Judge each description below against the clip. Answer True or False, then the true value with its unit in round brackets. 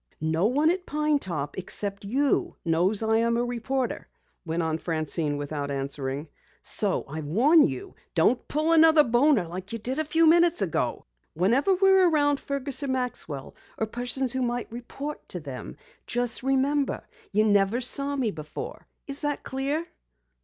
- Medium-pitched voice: False (240 Hz)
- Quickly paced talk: False (160 wpm)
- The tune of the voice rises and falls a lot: True (8.8 semitones)